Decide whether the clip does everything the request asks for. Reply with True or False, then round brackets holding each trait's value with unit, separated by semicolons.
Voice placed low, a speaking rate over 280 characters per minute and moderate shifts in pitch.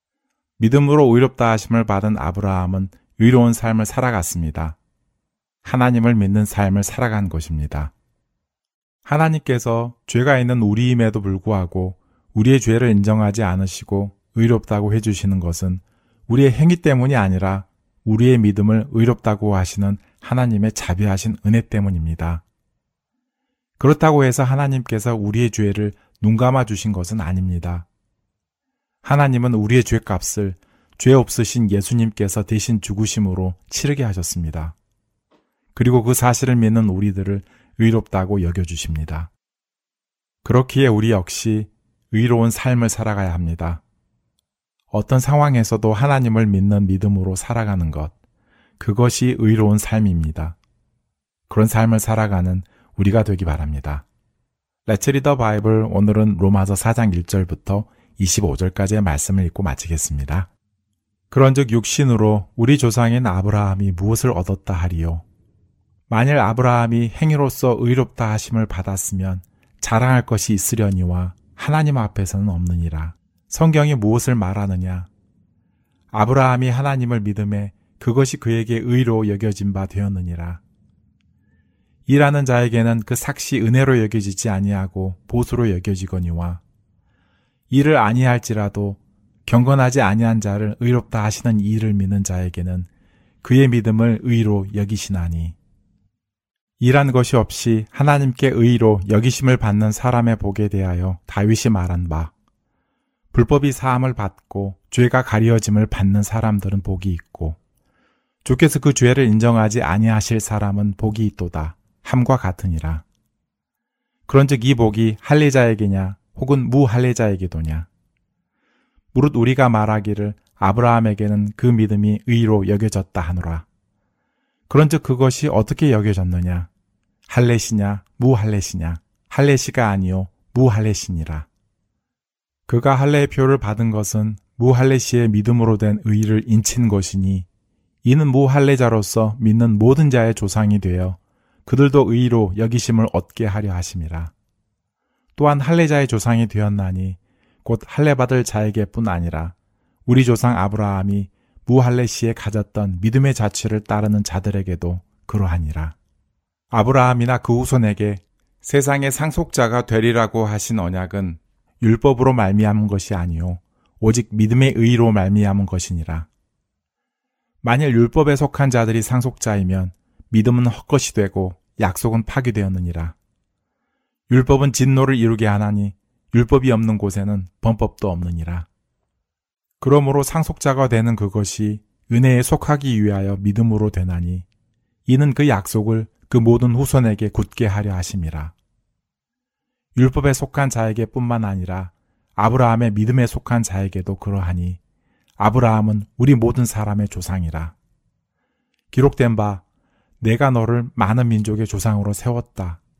True (110 Hz; 300 characters per minute; 4.0 semitones)